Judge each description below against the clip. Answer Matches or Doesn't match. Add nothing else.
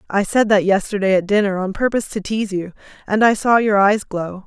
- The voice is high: Matches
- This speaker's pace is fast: Matches